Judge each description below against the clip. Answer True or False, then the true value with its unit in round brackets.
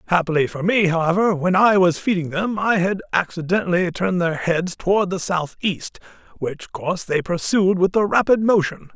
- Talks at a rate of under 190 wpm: True (175 wpm)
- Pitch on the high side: False (180 Hz)